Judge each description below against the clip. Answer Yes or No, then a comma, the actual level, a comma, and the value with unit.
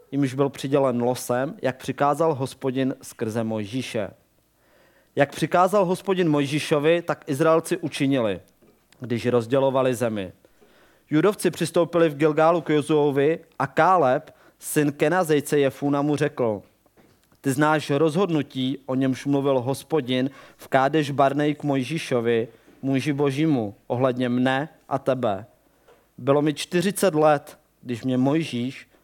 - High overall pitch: No, medium, 140 Hz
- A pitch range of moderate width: Yes, average, 3.3 semitones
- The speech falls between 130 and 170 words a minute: No, average, 120 wpm